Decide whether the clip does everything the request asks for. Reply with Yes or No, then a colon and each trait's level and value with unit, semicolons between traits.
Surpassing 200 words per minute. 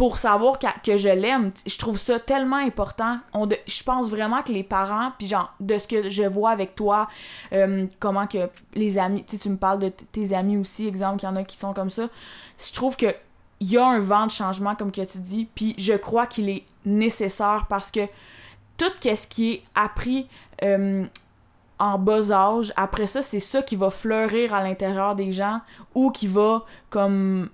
Yes: average, 210 wpm